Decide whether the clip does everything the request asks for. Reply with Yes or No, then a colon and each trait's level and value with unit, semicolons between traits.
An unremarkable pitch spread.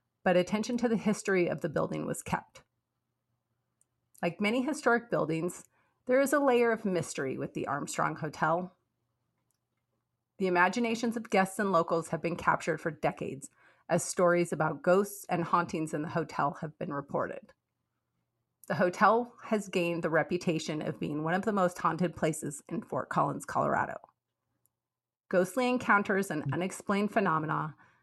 Yes: average, 4.5 semitones